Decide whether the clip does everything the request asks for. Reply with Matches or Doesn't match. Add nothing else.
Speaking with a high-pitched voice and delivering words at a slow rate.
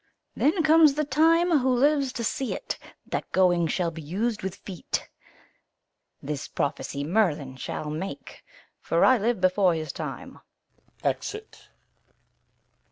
Matches